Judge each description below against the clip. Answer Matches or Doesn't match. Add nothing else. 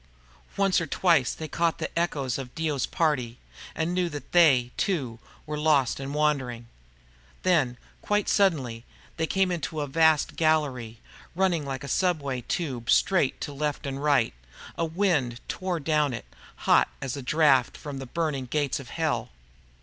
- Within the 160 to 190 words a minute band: Matches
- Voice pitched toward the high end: Doesn't match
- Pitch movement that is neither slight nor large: Matches